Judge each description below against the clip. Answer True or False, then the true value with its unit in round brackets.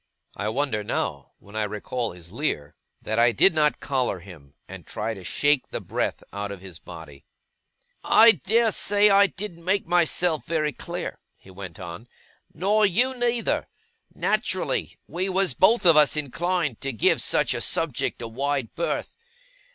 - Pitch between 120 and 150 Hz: True (140 Hz)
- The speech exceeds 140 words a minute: True (165 wpm)